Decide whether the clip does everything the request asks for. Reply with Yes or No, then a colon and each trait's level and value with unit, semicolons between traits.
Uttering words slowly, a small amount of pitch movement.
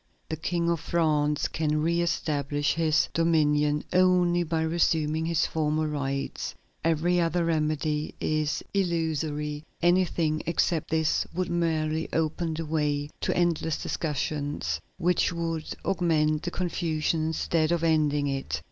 Yes: slow, 130 wpm; narrow, 2.0 semitones